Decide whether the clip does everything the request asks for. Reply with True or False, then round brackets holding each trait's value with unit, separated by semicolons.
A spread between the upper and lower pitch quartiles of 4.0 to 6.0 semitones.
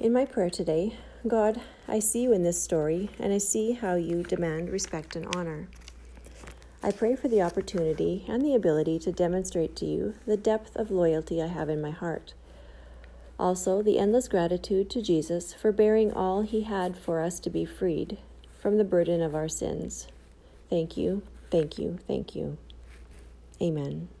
True (5.1 semitones)